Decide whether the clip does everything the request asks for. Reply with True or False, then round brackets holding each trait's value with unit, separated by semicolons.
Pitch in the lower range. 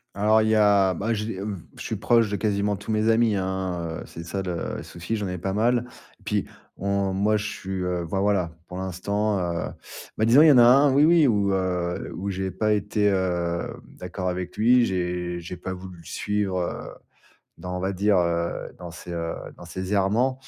True (95 Hz)